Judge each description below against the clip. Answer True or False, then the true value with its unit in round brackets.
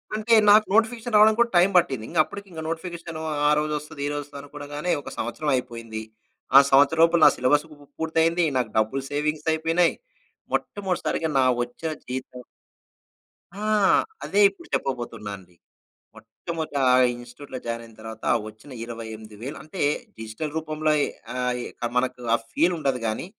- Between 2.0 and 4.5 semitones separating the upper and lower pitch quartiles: False (5.2 semitones)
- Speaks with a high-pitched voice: False (145 Hz)